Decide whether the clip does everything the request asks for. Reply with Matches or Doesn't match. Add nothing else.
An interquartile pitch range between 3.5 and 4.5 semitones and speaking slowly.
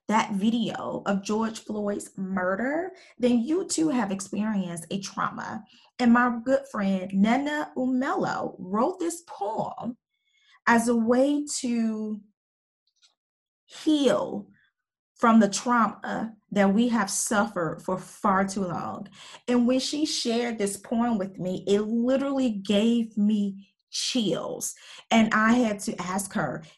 Matches